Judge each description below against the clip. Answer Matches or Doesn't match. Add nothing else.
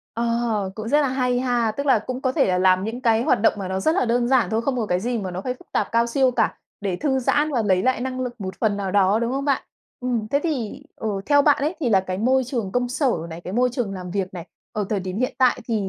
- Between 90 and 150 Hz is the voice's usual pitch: Doesn't match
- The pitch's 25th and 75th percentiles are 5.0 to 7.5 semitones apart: Doesn't match